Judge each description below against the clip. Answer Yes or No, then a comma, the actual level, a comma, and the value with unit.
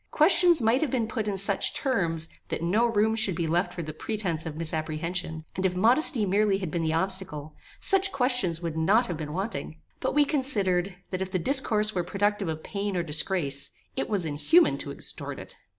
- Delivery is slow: No, average, 200 wpm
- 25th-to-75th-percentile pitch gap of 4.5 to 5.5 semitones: Yes, average, 5.2 semitones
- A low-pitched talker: No, high, 190 Hz